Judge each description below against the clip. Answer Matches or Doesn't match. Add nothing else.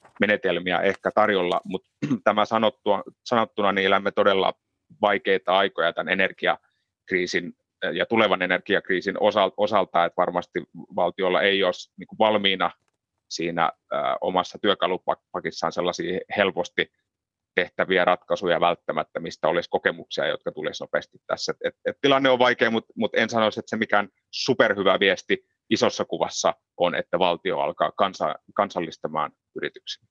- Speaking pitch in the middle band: Doesn't match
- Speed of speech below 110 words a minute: Doesn't match